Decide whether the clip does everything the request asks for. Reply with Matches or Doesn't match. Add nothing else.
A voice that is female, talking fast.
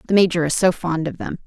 Matches